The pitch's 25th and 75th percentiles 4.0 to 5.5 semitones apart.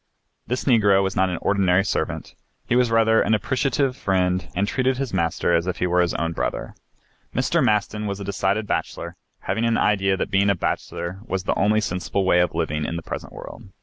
No: average, 3.4 semitones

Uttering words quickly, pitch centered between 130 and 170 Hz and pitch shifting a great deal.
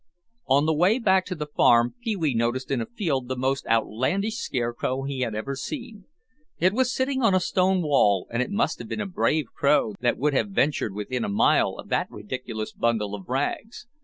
Yes: fast, 210 wpm; medium, 140 Hz; wide, 8.1 semitones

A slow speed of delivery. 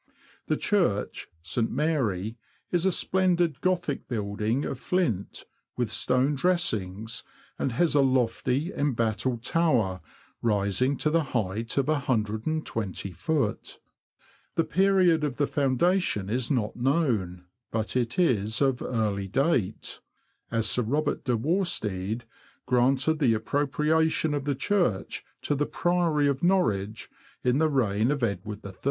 Yes: slow, 130 wpm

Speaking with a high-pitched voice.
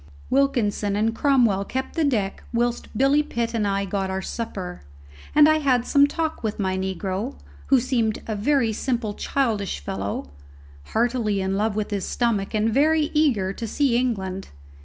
Yes: high, 225 Hz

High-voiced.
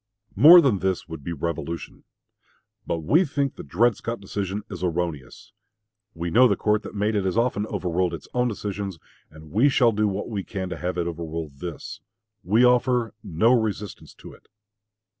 No: low, 100 Hz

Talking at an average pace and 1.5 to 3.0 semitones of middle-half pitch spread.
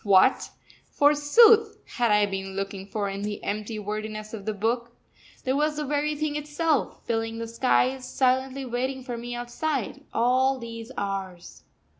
No: average, 155 wpm; average, 4.2 semitones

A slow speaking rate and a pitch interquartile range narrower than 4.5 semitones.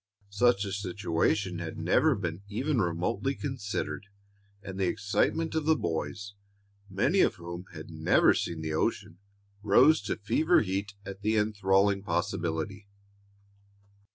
Yes: slow, 130 wpm; average, 3.8 semitones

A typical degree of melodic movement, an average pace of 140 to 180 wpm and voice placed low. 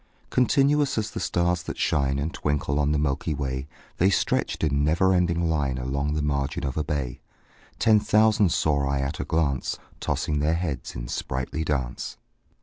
Yes: average, 3.9 semitones; average, 175 wpm; very low, 75 Hz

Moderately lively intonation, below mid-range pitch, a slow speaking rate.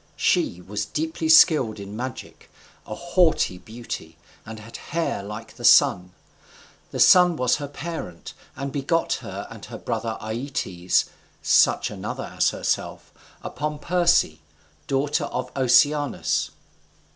No: wide, 6.3 semitones; low, 130 Hz; slow, 125 wpm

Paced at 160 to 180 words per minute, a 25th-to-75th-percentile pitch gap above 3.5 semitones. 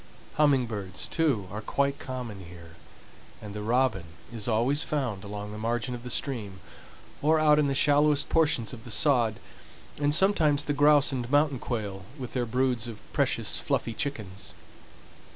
Yes: average, 165 wpm; average, 5.2 semitones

